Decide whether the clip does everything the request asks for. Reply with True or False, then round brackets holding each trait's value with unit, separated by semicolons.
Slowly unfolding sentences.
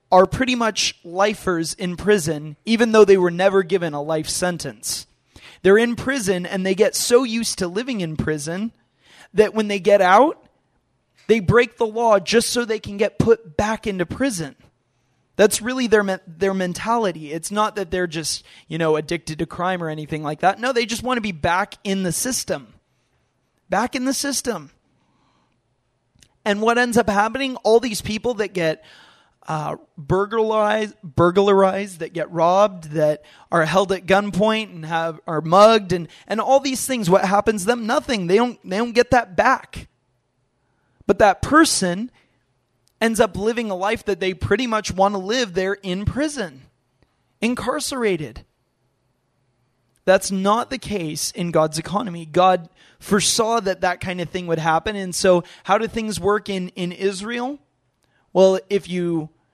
False (170 wpm)